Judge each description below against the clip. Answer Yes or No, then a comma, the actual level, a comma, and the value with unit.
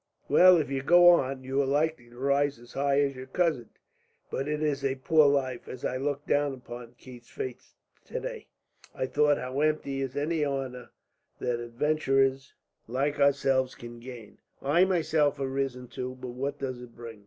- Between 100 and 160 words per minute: No, average, 180 wpm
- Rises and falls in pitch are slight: Yes, narrow, 2.3 semitones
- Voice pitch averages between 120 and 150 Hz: Yes, low, 135 Hz